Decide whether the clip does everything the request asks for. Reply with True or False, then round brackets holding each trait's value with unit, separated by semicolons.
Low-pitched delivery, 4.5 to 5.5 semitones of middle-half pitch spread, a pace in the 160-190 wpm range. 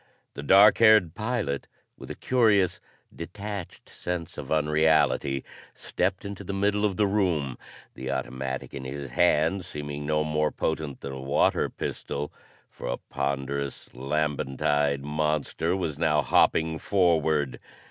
False (75 Hz; 4.8 semitones; 135 wpm)